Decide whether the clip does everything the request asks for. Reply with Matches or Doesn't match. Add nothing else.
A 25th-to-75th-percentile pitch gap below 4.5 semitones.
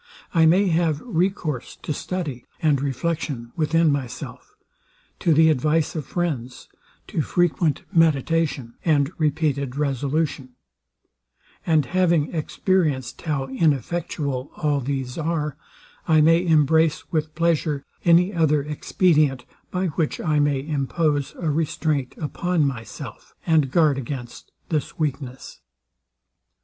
Matches